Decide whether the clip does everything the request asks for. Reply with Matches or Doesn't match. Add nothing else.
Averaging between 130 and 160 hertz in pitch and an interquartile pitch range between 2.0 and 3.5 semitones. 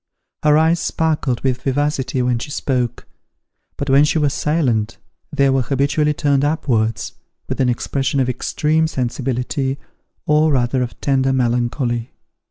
Matches